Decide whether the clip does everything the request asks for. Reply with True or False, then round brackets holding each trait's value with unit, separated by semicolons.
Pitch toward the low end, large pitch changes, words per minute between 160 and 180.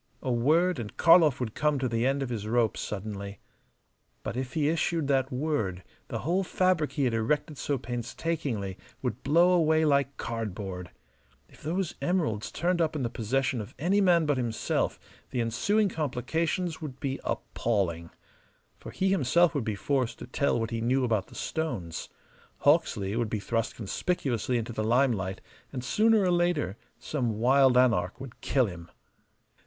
True (130 Hz; 5.9 semitones; 170 wpm)